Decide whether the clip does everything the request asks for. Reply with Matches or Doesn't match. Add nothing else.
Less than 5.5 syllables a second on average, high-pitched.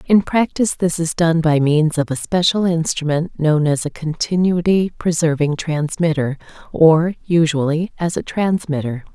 Doesn't match